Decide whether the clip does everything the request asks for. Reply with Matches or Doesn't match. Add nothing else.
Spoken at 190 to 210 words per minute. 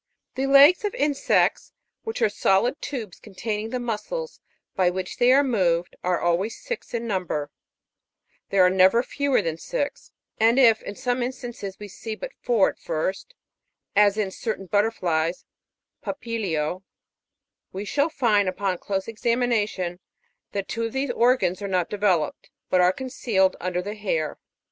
Doesn't match